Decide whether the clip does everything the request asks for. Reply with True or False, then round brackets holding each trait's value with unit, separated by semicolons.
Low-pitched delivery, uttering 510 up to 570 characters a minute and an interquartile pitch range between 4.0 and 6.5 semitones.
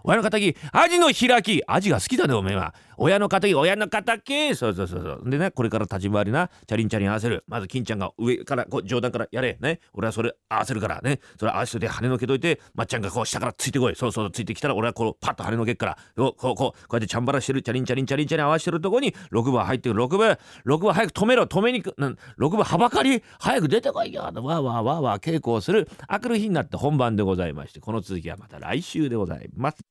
False (125 Hz; 515 characters per minute; 7.9 semitones)